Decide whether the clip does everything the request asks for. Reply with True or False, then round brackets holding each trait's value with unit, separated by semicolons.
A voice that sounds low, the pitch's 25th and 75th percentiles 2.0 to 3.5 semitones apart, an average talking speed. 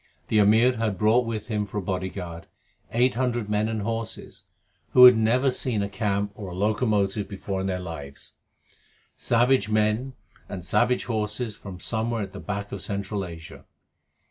True (105 Hz; 2.6 semitones; 170 wpm)